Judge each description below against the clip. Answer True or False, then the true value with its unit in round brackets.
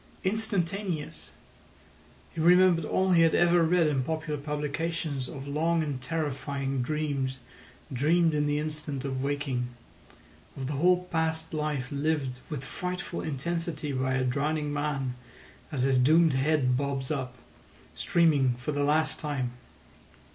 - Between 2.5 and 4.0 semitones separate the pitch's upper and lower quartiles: True (3.2 semitones)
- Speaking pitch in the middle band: True (150 Hz)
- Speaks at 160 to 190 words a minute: False (135 wpm)